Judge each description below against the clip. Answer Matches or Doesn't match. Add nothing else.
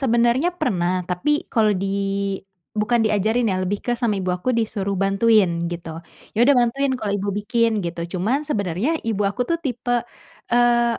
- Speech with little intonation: Doesn't match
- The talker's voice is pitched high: Matches